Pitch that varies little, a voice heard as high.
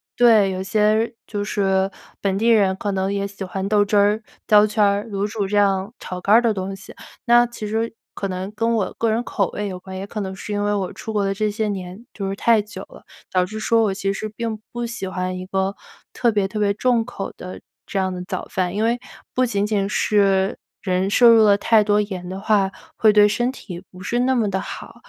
Yes: narrow, 2.2 semitones; high, 205 Hz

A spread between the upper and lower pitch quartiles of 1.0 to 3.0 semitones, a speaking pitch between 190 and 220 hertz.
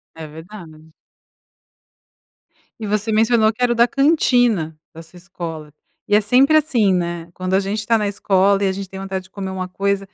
No: average, 3.6 semitones; high, 195 Hz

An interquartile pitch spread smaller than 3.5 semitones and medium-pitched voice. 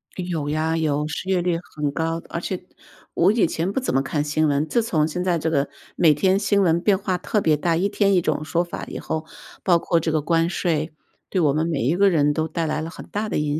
Yes: average, 3.0 semitones; medium, 165 Hz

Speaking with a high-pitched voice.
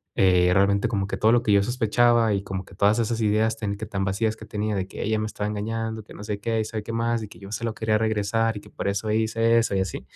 No: low, 110 Hz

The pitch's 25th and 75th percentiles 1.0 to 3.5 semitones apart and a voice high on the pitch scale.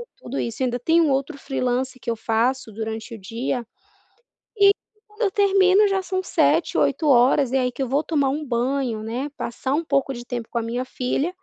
No: average, 4.2 semitones; very high, 260 Hz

